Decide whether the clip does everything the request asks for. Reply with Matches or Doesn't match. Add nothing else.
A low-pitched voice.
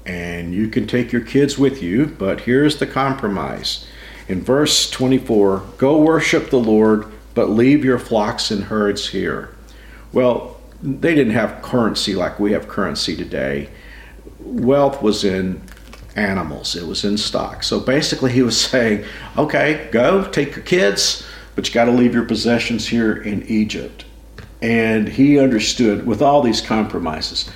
Matches